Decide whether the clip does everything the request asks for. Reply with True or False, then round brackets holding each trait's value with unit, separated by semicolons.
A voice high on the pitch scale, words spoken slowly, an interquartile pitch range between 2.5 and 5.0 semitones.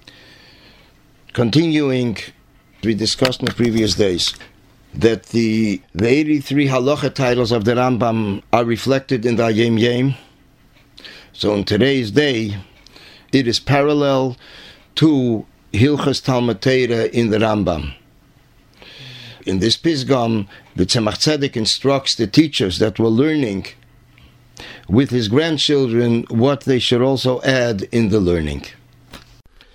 False (125 Hz; 115 wpm; 3.5 semitones)